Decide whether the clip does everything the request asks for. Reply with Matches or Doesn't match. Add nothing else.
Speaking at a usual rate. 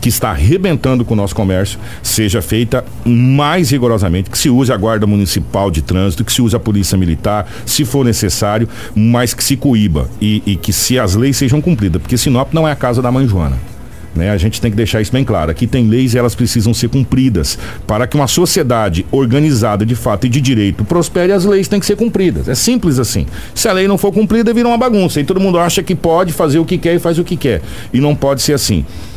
Doesn't match